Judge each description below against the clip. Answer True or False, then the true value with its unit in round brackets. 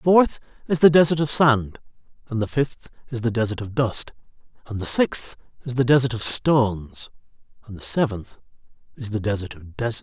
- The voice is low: True (120 Hz)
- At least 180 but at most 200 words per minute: True (185 wpm)